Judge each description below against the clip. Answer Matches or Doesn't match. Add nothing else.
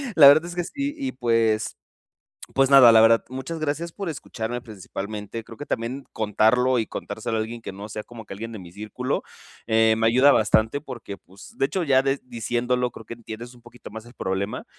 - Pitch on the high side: Doesn't match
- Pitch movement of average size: Matches